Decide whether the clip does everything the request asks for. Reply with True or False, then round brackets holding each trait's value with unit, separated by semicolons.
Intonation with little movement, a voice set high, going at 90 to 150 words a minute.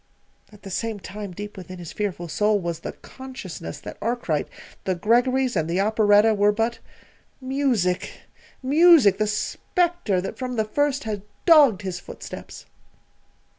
False (5.1 semitones; 215 Hz; 145 wpm)